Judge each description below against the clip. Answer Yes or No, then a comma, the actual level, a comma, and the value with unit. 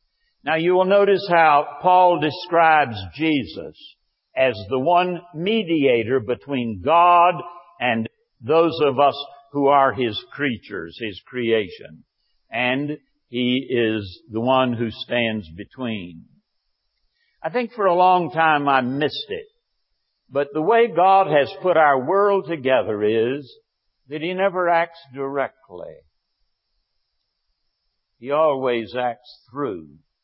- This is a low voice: No, medium, 145 Hz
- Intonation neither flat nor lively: No, wide, 6.1 semitones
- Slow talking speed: Yes, slow, 120 wpm